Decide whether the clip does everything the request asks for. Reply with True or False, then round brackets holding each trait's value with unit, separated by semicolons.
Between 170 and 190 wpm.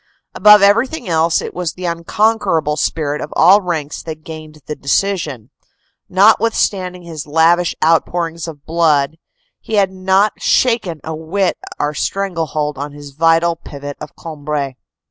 False (150 wpm)